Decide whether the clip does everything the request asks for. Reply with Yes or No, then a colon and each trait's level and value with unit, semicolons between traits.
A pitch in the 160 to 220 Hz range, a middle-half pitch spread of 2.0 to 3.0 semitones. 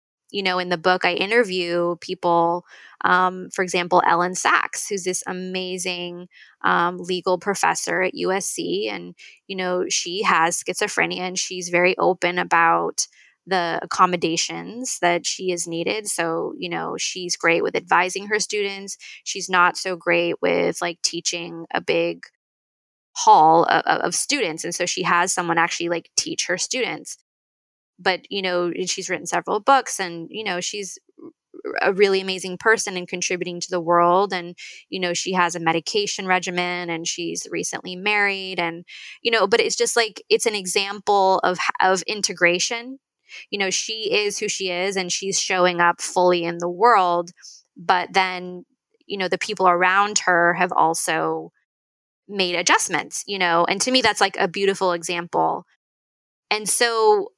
Yes: medium, 185 Hz; narrow, 2.4 semitones